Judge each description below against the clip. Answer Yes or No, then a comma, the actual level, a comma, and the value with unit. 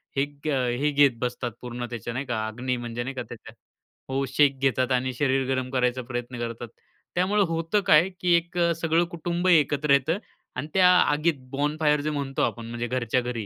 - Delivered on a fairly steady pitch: No, average, 3.9 semitones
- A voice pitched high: No, low, 135 Hz